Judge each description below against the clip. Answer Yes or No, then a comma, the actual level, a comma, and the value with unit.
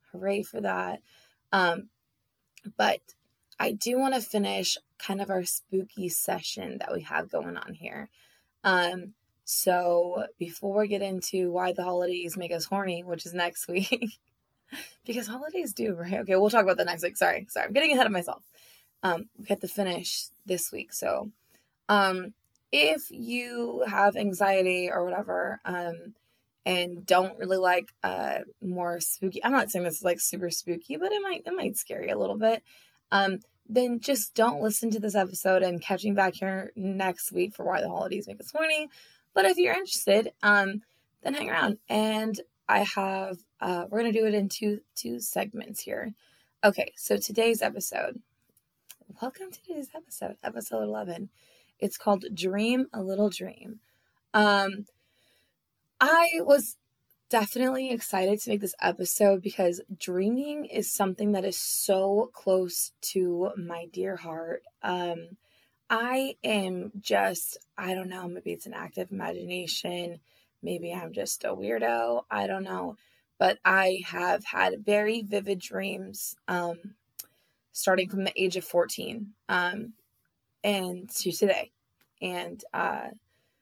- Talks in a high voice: Yes, high, 195 Hz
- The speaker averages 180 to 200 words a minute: No, average, 155 wpm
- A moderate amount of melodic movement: Yes, average, 3.6 semitones